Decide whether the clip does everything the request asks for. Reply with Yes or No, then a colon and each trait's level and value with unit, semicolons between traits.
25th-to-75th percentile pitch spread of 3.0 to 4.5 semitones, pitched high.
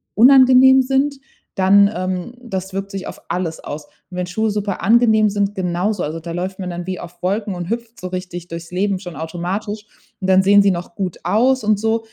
Yes: average, 3.4 semitones; high, 195 Hz